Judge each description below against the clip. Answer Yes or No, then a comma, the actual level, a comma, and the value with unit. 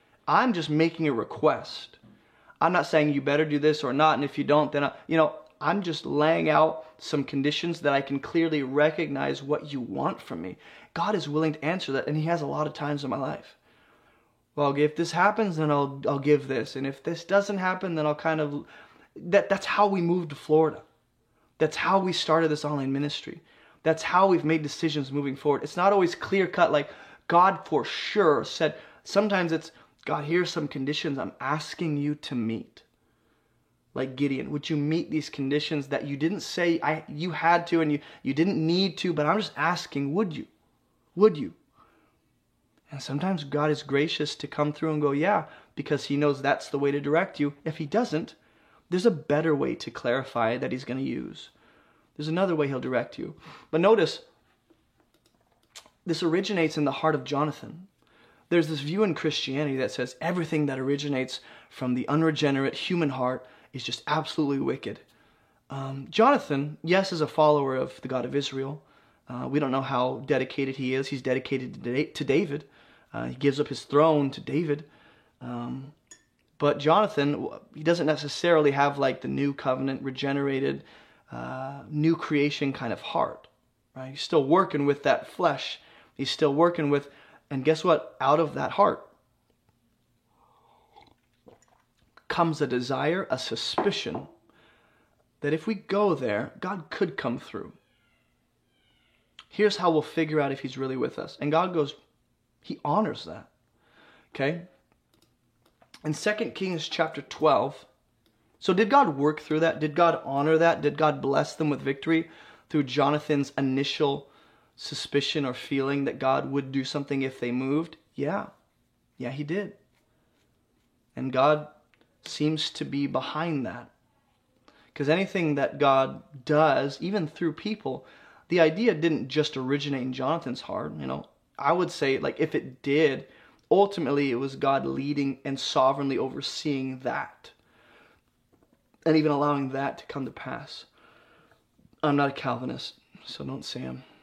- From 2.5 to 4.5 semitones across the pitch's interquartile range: Yes, average, 2.9 semitones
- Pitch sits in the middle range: Yes, medium, 150 Hz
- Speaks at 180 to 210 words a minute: No, average, 170 wpm